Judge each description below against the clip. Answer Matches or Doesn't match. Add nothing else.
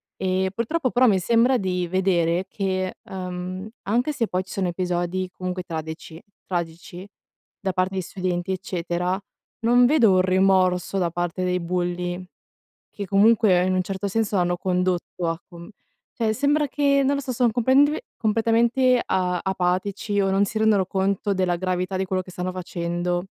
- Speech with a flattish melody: Doesn't match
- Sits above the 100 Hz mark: Matches